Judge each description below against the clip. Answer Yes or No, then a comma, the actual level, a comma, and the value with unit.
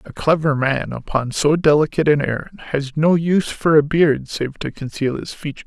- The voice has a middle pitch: Yes, medium, 150 Hz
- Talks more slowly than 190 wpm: No, average, 200 wpm